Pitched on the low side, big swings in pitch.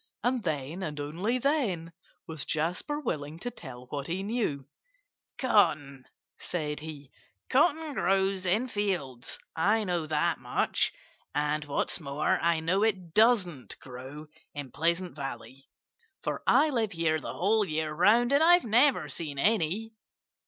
No: medium, 170 Hz; wide, 6.8 semitones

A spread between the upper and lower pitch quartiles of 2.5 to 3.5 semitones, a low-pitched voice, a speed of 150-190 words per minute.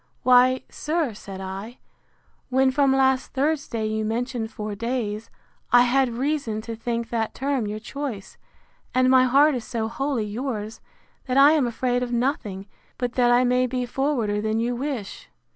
No: average, 3.1 semitones; high, 245 Hz; average, 165 wpm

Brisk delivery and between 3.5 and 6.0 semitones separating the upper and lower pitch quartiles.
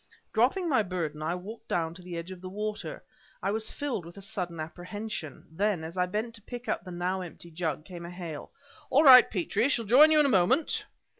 Yes: fast, 225 wpm; average, 4.7 semitones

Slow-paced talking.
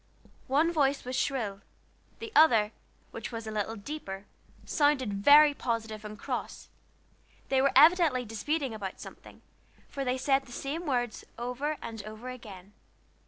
No: average, 145 wpm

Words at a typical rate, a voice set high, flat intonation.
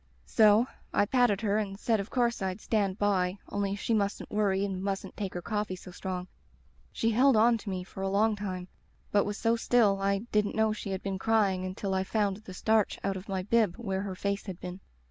No: fast, 220 wpm; high, 200 Hz; narrow, 2.2 semitones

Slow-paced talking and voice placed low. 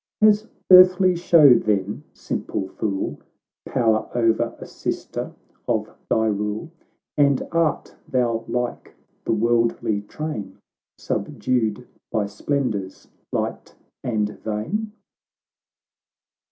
Yes: slow, 100 wpm; low, 115 Hz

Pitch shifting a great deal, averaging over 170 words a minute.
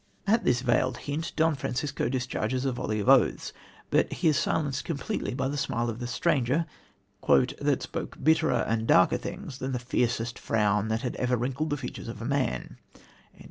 No: average, 3.1 semitones; average, 180 wpm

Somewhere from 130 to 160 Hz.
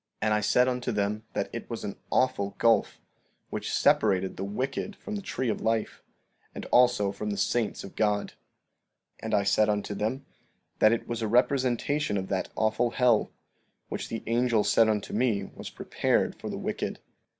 No: low, 110 Hz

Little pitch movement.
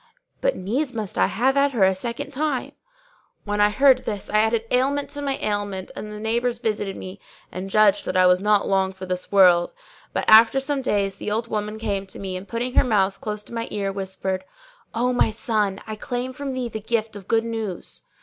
No: average, 3.8 semitones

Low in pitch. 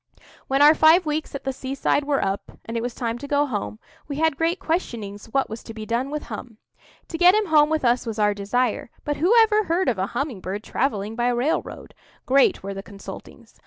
No: very high, 260 Hz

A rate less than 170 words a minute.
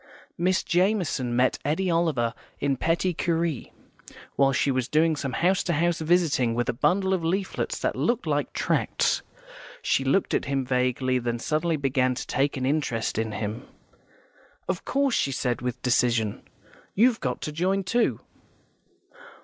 Yes: average, 155 wpm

